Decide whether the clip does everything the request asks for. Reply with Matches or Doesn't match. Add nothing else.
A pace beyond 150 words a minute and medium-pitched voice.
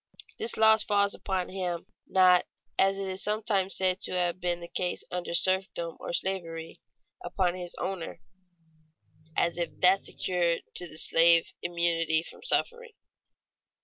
Doesn't match